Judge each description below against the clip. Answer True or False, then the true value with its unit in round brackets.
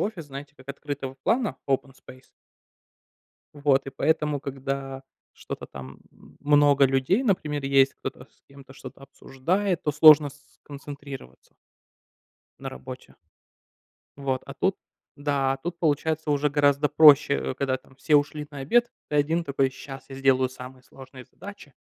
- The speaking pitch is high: False (140 Hz)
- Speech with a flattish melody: True (1.9 semitones)